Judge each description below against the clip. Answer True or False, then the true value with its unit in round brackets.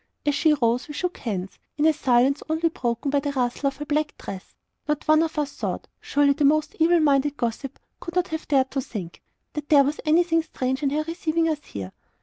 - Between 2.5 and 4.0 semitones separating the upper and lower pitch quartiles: True (2.9 semitones)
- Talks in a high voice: True (290 Hz)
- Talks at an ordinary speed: False (225 wpm)